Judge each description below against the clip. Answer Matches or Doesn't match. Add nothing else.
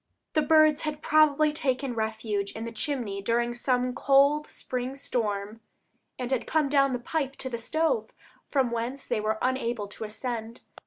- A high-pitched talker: Matches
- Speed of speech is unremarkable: Matches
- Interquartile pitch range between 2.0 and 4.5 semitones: Matches